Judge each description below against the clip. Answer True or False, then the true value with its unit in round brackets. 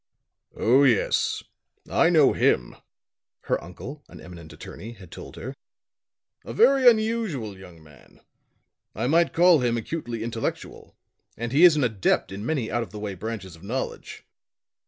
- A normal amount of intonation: False (7.4 semitones)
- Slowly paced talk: False (155 wpm)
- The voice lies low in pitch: True (115 Hz)